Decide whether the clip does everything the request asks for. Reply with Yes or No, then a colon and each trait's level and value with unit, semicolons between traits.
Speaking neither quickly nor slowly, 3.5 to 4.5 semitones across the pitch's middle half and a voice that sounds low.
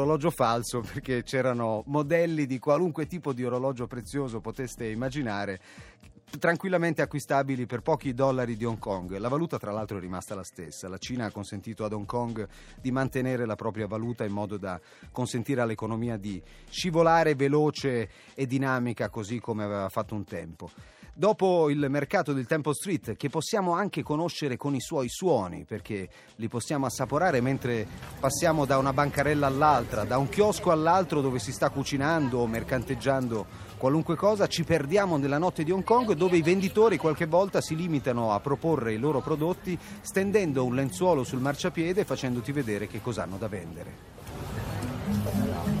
No: average, 160 wpm; wide, 5.6 semitones; low, 130 Hz